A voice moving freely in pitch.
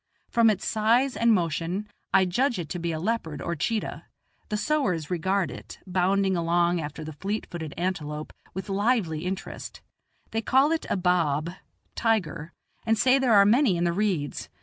No: average, 4.8 semitones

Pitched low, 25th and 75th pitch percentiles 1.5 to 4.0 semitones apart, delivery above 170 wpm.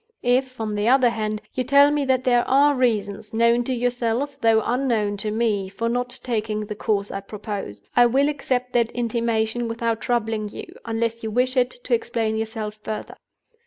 No: high, 230 Hz; narrow, 2.4 semitones; average, 185 wpm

